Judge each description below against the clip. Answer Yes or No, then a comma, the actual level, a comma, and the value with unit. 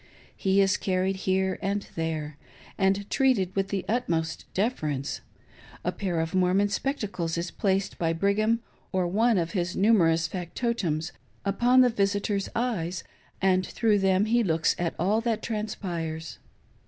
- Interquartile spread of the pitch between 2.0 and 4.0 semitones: Yes, average, 3.7 semitones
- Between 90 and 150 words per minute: Yes, average, 145 wpm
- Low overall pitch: No, high, 190 Hz